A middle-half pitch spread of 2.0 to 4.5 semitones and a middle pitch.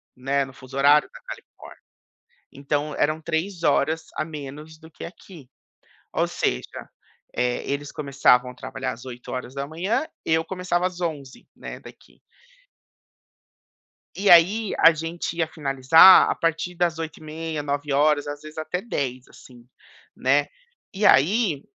Yes: average, 3.4 semitones; medium, 155 Hz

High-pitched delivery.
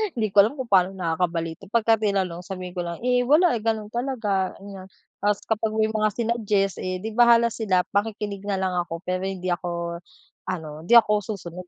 Yes: high, 200 Hz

